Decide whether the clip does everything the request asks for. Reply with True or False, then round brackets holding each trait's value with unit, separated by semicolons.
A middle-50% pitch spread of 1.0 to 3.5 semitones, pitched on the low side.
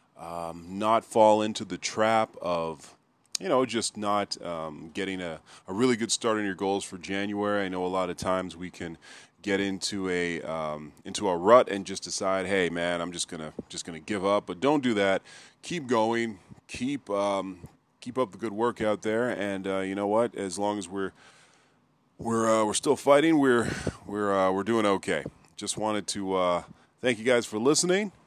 True (3.2 semitones; 100 Hz)